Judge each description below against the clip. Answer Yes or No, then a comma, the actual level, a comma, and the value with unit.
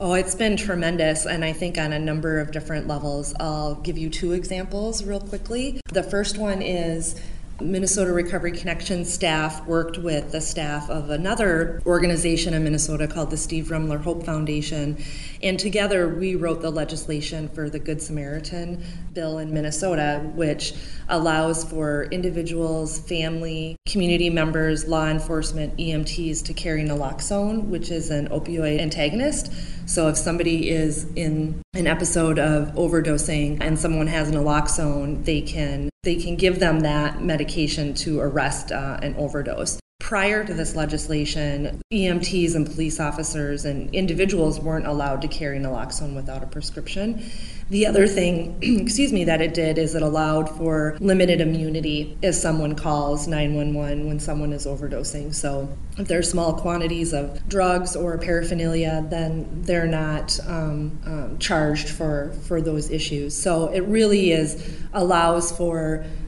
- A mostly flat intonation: Yes, narrow, 2.3 semitones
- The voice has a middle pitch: Yes, medium, 160 Hz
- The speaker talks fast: No, average, 150 wpm